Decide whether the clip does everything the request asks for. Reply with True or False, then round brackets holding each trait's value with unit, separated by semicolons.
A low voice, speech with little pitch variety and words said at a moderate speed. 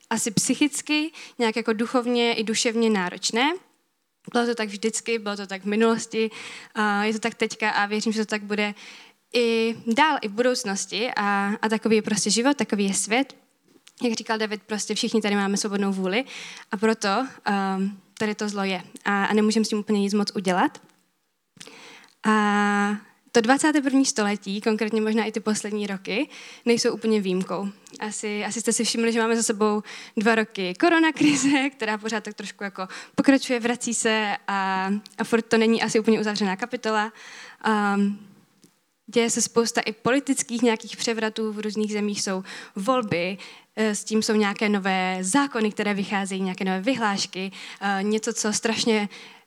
False (220 Hz; 2.3 semitones; 160 wpm)